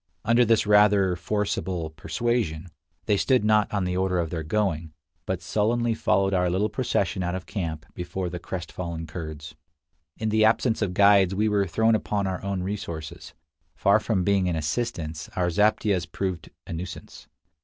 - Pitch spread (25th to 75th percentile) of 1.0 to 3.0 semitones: No, average, 3.4 semitones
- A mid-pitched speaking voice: No, very low, 95 Hz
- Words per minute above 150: Yes, average, 165 wpm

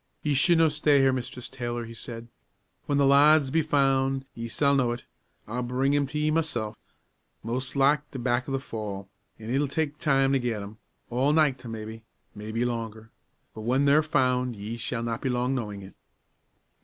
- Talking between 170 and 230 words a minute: Yes, average, 190 wpm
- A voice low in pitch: Yes, low, 130 Hz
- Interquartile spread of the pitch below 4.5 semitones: Yes, average, 3.4 semitones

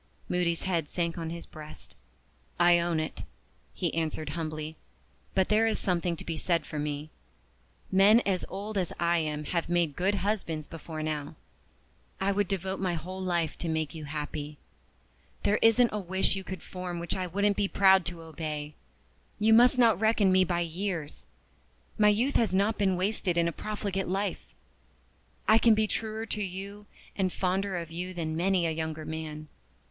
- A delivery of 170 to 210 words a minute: Yes, average, 180 wpm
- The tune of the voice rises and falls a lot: No, average, 3.6 semitones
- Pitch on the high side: No, medium, 180 Hz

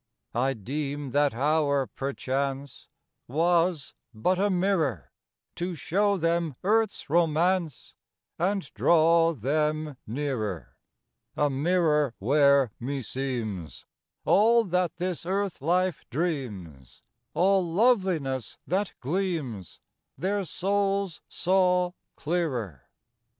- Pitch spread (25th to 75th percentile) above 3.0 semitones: Yes, average, 5.2 semitones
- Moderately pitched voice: Yes, medium, 155 Hz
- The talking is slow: Yes, slow, 95 wpm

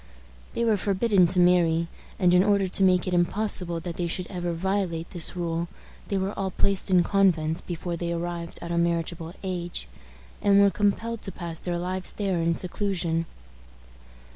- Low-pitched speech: No, medium, 180 Hz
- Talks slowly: No, average, 175 wpm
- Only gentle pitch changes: Yes, narrow, 2.3 semitones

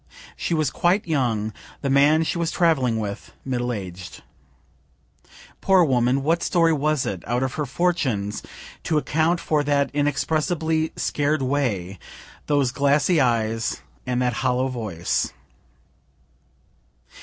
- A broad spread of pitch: No, average, 4.5 semitones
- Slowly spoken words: Yes, slow, 125 wpm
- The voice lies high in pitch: No, medium, 140 Hz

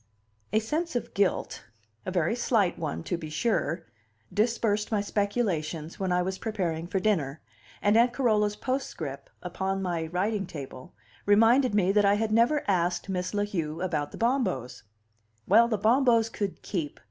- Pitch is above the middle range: Yes, high, 200 Hz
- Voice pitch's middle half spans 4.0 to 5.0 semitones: Yes, average, 4.6 semitones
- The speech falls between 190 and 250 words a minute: No, average, 165 wpm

